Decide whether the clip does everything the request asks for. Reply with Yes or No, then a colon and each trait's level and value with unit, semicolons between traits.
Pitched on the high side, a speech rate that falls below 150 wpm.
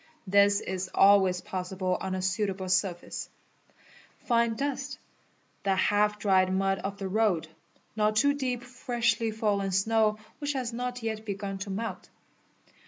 Yes: high, 205 Hz; average, 140 wpm